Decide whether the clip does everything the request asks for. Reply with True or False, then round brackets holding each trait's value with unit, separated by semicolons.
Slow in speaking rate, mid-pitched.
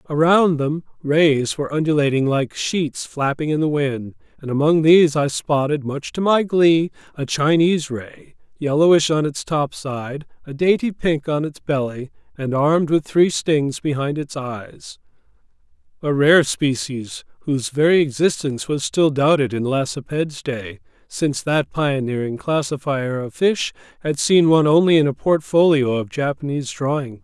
False (150 wpm; 145 Hz)